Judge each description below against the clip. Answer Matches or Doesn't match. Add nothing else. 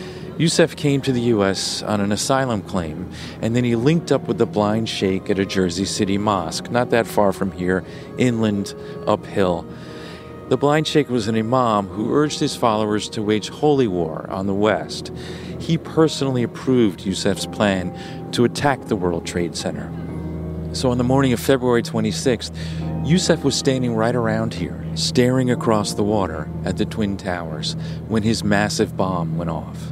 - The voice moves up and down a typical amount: Doesn't match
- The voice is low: Matches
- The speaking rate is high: Doesn't match